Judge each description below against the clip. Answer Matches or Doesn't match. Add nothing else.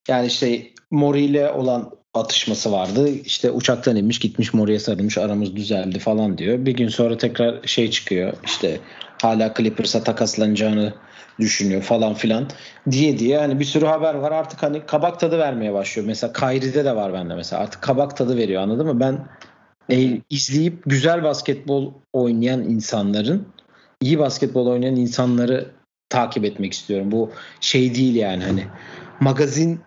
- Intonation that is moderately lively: Matches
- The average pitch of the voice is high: Doesn't match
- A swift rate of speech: Matches